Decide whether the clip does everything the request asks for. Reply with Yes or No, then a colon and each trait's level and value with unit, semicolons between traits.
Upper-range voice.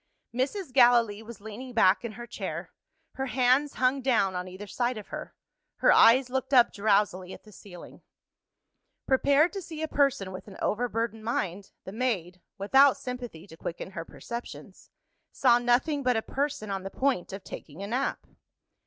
Yes: high, 235 Hz